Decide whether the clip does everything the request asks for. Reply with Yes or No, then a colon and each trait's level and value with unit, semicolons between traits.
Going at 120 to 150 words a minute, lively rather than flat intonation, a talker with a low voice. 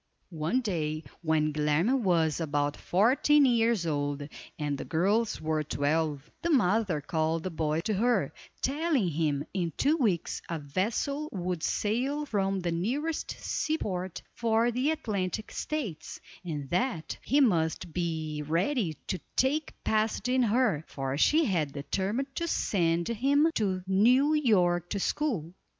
No: average, 145 wpm; wide, 7.6 semitones; medium, 185 Hz